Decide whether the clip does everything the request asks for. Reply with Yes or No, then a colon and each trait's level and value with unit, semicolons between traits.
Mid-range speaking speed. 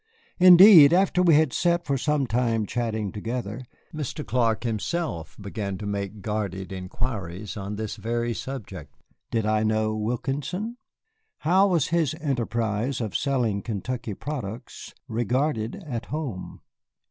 No: slow, 130 wpm